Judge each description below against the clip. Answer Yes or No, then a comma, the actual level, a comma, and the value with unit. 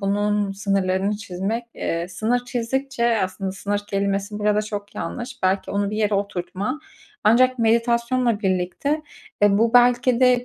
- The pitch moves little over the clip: No, average, 3.5 semitones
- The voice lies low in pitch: No, high, 210 Hz